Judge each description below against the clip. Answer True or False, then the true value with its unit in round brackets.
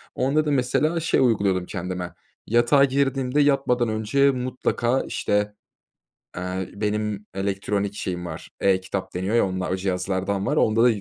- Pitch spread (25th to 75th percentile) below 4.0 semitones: False (5.2 semitones)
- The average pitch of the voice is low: True (105 Hz)